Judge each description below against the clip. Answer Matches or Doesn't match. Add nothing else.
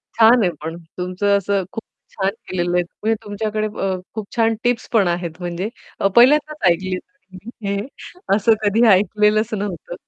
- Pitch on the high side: Matches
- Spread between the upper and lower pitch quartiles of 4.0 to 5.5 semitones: Doesn't match